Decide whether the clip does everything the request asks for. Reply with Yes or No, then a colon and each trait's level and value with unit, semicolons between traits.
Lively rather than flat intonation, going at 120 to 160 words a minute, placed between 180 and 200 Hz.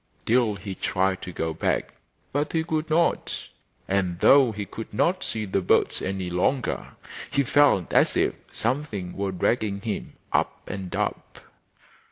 No: wide, 6.7 semitones; average, 155 wpm; low, 105 Hz